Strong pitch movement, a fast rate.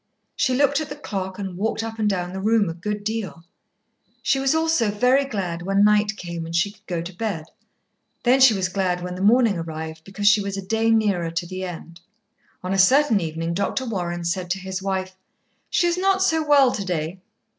No: average, 4.2 semitones; fast, 215 wpm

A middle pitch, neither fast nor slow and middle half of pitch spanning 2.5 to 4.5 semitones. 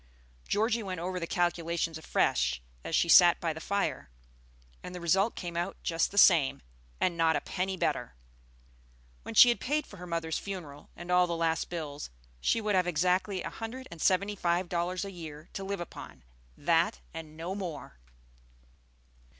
Yes: medium, 175 Hz; average, 175 wpm; average, 2.8 semitones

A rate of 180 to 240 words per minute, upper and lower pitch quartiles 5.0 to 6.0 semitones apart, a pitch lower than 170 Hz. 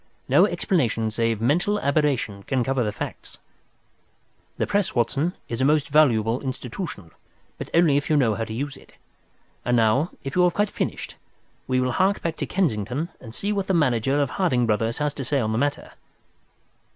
Yes: average, 185 wpm; wide, 5.5 semitones; low, 135 Hz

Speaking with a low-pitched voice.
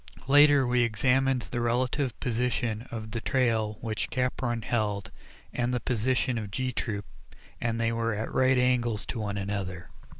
Yes: low, 120 Hz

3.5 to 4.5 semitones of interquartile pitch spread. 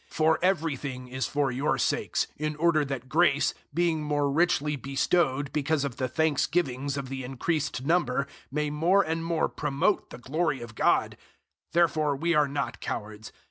No: average, 3.1 semitones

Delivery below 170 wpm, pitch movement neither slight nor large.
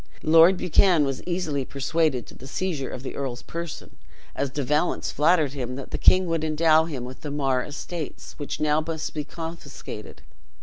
No: average, 180 wpm; average, 3.2 semitones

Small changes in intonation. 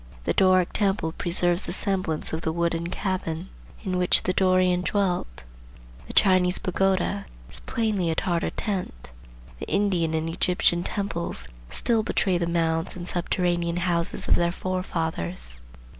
Yes: narrow, 2.0 semitones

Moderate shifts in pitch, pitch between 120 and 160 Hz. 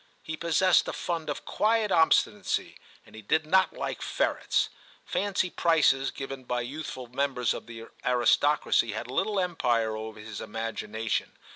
No: wide, 6.5 semitones; low, 135 Hz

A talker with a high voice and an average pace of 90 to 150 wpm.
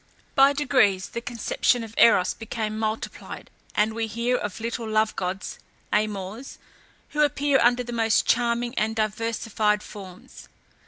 Yes: high, 225 Hz; average, 140 wpm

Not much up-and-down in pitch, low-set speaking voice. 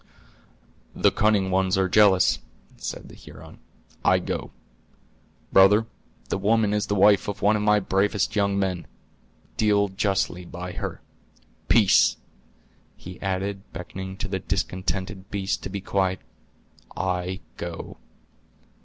Yes: narrow, 1.6 semitones; very low, 95 Hz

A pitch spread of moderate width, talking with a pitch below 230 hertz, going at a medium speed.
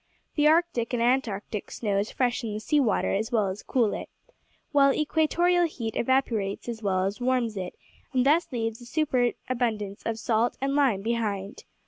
No: average, 4.2 semitones; high, 235 Hz; average, 165 wpm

